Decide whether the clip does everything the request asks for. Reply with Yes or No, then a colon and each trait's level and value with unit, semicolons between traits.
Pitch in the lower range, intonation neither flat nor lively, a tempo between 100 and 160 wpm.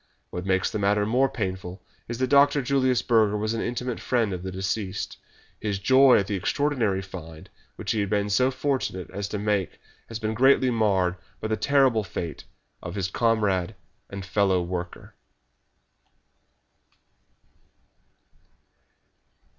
Yes: low, 105 Hz; average, 4.5 semitones; average, 145 wpm